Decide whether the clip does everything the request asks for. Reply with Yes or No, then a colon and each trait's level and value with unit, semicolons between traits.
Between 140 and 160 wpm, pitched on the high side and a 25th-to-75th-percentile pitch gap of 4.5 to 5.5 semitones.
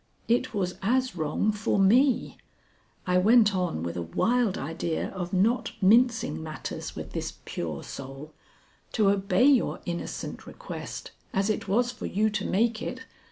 Yes: average, 155 wpm; high, 200 Hz; average, 5.2 semitones